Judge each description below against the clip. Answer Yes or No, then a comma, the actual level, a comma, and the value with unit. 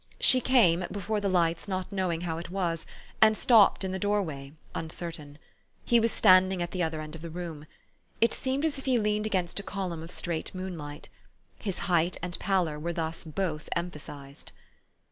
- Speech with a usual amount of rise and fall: Yes, average, 3.6 semitones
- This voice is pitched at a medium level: Yes, medium, 180 Hz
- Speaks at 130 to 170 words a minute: No, average, 185 wpm